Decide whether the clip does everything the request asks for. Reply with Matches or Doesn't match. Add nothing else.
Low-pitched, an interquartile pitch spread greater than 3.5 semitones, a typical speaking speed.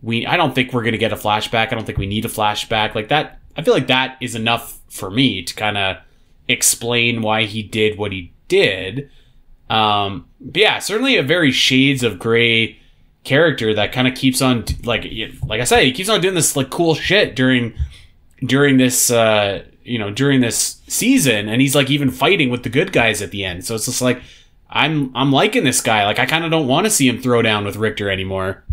Doesn't match